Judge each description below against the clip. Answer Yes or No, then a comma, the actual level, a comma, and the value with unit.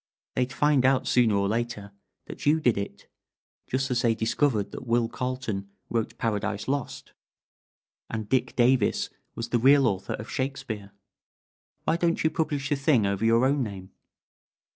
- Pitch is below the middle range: Yes, low, 120 Hz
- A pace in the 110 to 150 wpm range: No, average, 160 wpm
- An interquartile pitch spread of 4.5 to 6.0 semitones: No, average, 3.7 semitones